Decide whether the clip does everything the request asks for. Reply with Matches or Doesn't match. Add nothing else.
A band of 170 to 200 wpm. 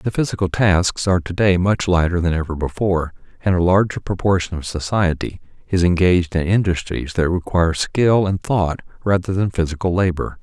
Matches